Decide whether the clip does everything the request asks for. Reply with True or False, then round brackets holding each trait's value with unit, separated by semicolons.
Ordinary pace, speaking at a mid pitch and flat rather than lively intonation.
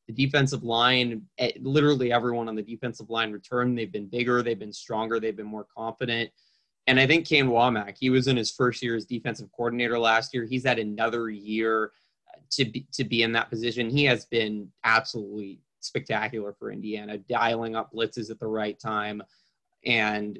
False (180 wpm; 115 Hz; 2.1 semitones)